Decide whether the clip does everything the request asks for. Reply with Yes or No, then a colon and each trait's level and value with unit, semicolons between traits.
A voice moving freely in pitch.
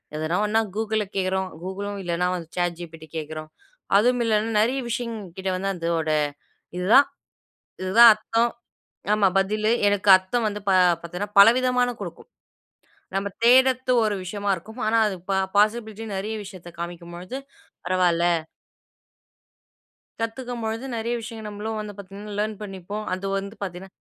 No: average, 3.4 semitones